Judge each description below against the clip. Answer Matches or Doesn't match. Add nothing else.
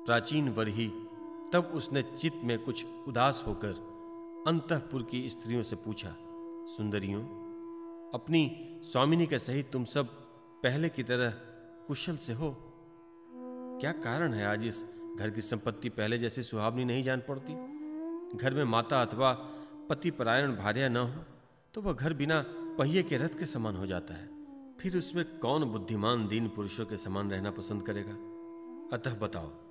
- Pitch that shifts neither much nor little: Doesn't match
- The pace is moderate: Matches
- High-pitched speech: Doesn't match